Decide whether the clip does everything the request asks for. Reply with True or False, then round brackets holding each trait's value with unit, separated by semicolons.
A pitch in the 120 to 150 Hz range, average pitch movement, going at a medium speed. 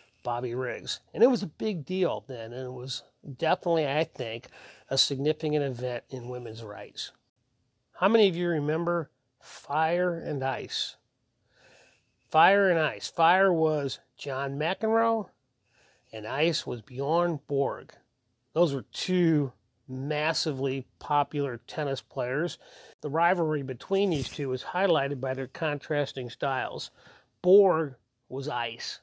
False (140 Hz; 4.4 semitones; 130 wpm)